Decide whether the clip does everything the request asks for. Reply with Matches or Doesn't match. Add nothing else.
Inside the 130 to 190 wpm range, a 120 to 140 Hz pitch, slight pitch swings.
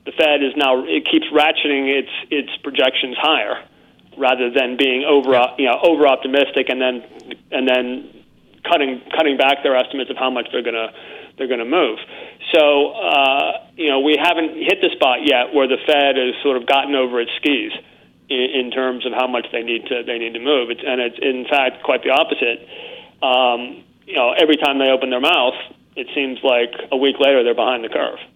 Doesn't match